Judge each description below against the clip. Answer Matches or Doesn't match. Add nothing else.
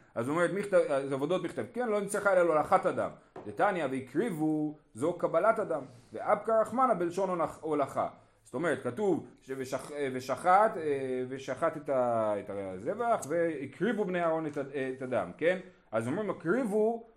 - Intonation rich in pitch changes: Matches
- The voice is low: Doesn't match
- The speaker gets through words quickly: Doesn't match